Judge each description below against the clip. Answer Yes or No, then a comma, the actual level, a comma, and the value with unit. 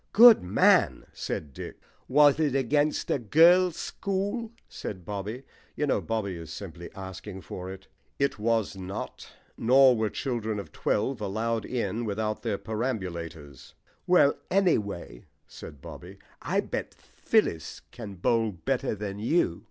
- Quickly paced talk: No, slow, 135 wpm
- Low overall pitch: Yes, low, 110 Hz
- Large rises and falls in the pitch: Yes, wide, 6.1 semitones